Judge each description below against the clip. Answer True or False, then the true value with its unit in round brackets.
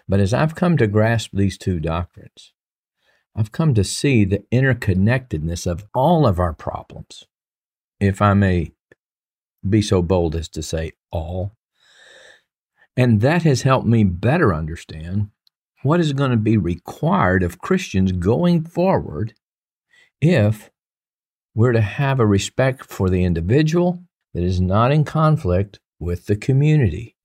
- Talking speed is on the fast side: False (140 wpm)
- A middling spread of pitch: False (6.4 semitones)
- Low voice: True (105 Hz)